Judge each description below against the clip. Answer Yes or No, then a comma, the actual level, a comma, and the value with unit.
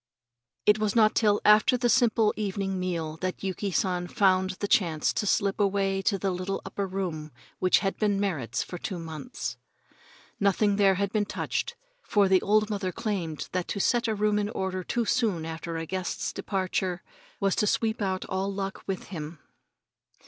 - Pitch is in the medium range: No, high, 195 Hz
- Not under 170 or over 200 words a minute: Yes, average, 180 wpm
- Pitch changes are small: Yes, narrow, 2.3 semitones